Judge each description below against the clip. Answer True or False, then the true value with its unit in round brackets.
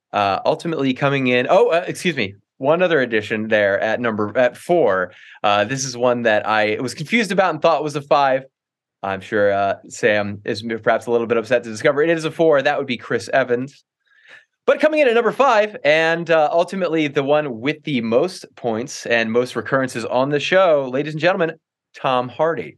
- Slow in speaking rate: False (205 wpm)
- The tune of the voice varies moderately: False (5.7 semitones)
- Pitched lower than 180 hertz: True (135 Hz)